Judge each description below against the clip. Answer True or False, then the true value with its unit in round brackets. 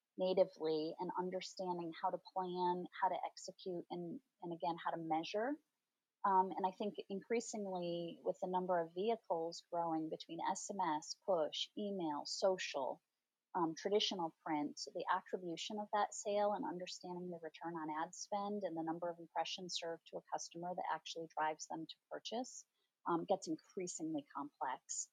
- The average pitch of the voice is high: False (180 Hz)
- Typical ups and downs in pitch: True (3.5 semitones)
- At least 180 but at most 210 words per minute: False (155 wpm)